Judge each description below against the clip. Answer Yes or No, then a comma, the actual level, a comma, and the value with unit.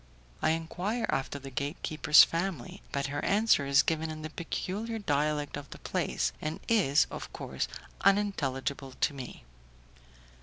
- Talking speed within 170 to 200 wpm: No, average, 145 wpm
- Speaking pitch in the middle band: Yes, medium, 155 Hz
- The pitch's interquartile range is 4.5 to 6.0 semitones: Yes, average, 5.0 semitones